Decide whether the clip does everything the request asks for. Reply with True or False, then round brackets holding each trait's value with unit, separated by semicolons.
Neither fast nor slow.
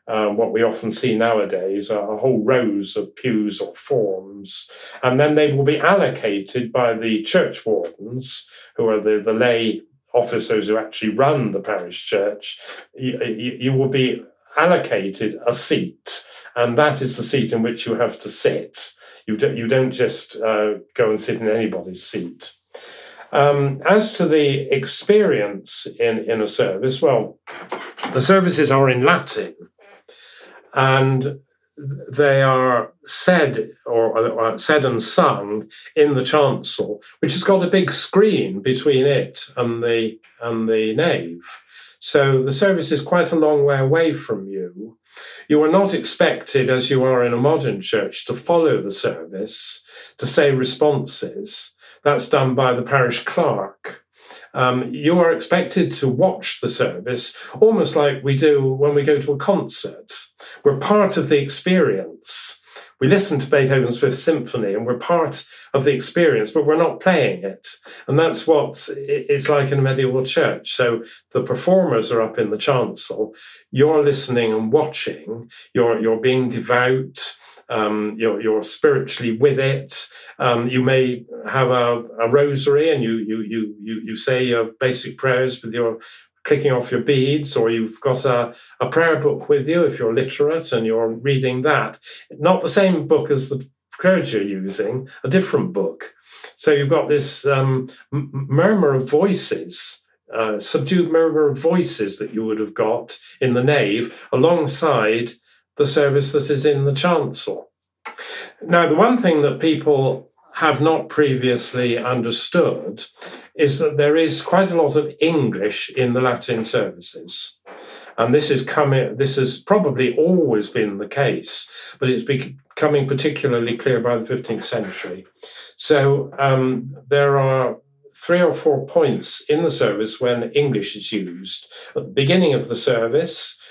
True (160 wpm)